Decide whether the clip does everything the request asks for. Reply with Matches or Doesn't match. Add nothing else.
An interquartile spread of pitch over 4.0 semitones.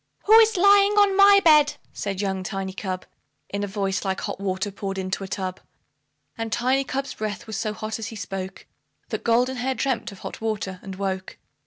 Matches